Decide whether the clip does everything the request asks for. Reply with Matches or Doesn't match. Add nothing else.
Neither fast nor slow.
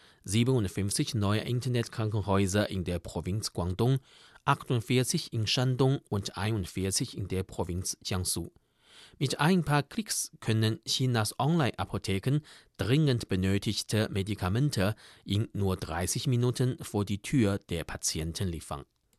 Doesn't match